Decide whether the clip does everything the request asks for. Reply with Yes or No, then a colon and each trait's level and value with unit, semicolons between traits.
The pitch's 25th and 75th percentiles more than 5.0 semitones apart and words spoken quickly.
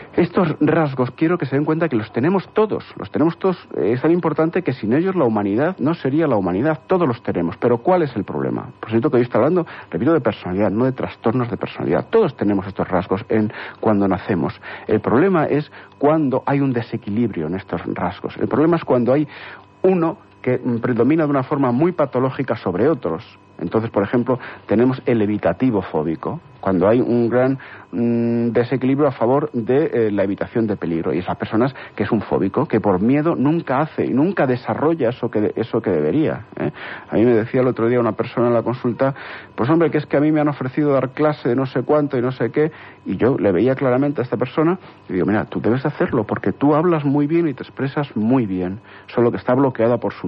Yes: wide, 5.5 semitones; fast, 220 wpm